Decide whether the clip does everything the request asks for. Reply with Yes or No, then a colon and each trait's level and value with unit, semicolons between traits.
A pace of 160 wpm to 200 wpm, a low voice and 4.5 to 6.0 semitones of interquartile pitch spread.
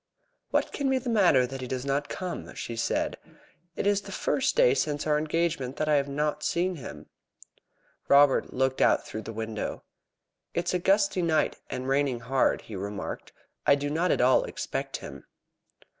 No: average, 185 wpm; medium, 145 Hz; average, 5.1 semitones